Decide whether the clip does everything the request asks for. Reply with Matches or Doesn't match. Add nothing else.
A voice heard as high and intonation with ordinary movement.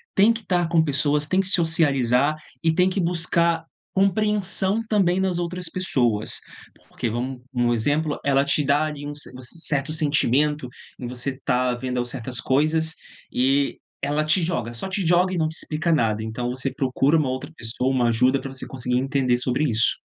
Doesn't match